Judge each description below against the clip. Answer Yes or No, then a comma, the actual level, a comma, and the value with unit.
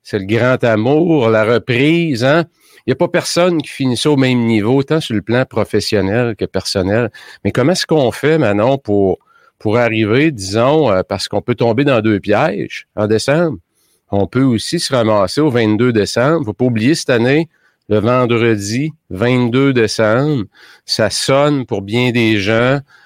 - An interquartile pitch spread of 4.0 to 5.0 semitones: Yes, average, 4.7 semitones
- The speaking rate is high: No, average, 170 wpm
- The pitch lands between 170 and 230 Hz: No, low, 125 Hz